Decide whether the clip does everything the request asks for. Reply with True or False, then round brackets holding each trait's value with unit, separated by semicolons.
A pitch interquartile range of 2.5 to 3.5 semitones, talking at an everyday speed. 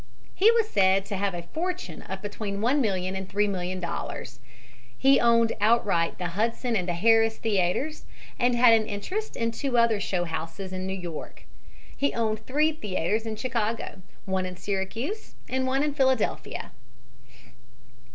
False (4.5 semitones; 150 wpm)